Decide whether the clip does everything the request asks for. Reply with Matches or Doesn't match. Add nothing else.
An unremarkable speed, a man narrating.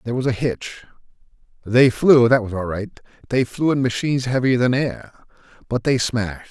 Matches